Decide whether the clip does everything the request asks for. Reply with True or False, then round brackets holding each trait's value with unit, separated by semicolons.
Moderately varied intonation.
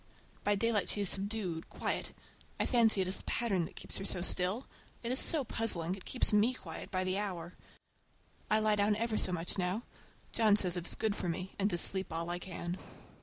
True (3.3 semitones)